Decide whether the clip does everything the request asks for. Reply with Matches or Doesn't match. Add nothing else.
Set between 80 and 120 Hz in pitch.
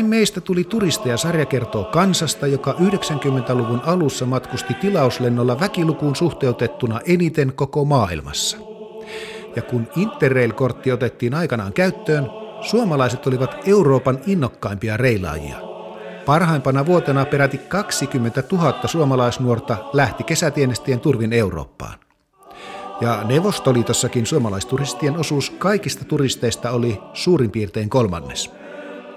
Doesn't match